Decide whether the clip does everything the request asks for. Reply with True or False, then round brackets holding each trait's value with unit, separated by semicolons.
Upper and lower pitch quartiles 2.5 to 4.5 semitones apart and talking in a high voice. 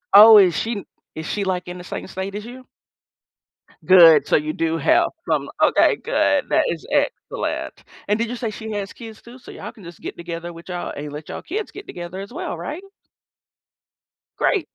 False (5.2 semitones; 195 Hz)